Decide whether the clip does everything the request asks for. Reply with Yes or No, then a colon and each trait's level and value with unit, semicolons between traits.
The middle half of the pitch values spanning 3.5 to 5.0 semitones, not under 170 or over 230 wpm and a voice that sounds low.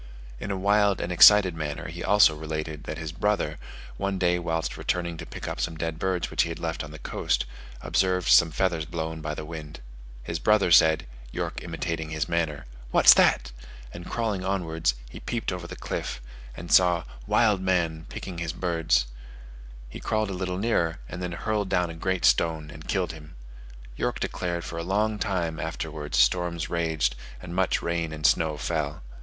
No: average, 2.8 semitones; average, 185 wpm; very low, 85 Hz